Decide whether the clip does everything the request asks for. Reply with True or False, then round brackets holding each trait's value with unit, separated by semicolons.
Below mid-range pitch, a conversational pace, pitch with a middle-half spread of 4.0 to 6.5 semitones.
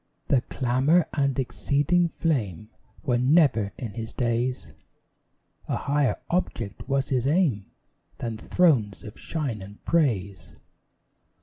False (130 Hz; 115 wpm; 4.9 semitones)